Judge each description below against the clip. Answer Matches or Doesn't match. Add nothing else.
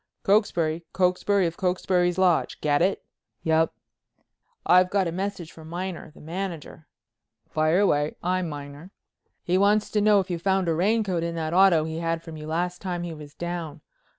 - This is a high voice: Doesn't match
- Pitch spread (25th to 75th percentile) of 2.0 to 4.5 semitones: Matches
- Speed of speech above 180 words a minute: Doesn't match